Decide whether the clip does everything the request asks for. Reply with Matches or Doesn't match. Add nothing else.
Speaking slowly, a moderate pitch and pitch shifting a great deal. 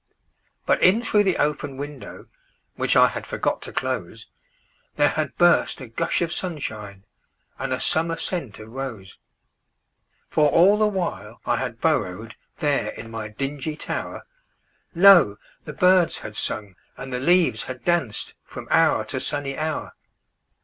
Matches